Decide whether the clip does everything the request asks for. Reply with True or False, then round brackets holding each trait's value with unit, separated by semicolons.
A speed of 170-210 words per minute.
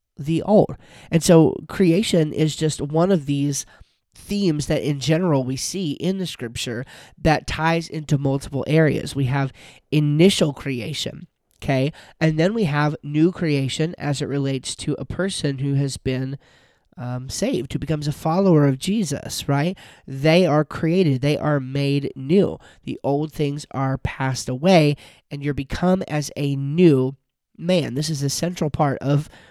False (160 wpm)